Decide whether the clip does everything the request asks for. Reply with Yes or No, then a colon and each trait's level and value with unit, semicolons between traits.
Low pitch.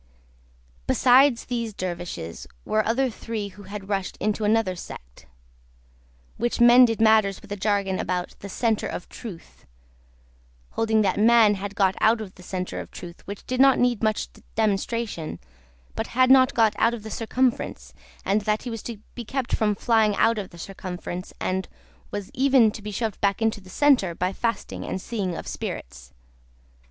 No: high, 215 Hz